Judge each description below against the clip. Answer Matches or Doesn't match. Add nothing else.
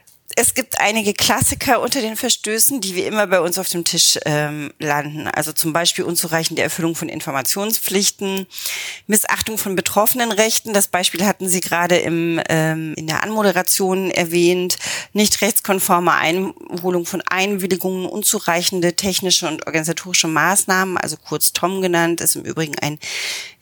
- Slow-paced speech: Doesn't match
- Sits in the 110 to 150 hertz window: Doesn't match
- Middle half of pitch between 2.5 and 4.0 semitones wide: Matches